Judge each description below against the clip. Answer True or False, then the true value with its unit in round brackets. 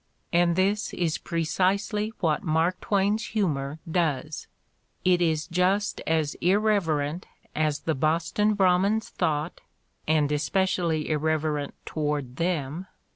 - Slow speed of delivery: True (115 wpm)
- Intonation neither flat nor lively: True (3.7 semitones)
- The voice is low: False (165 Hz)